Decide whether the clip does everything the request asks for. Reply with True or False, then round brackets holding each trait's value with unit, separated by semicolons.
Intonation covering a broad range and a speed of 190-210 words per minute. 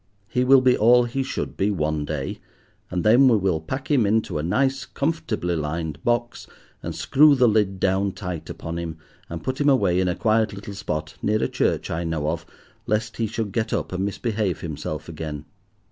True (6.2 semitones; 200 wpm)